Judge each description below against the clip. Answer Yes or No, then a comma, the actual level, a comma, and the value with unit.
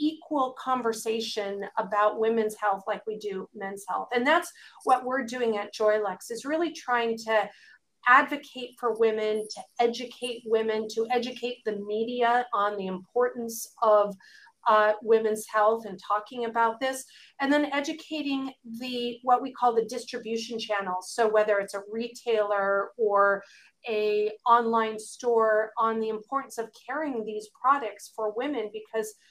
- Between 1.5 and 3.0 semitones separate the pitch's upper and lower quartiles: Yes, narrow, 2.5 semitones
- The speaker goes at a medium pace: Yes, average, 145 wpm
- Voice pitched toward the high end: Yes, high, 225 Hz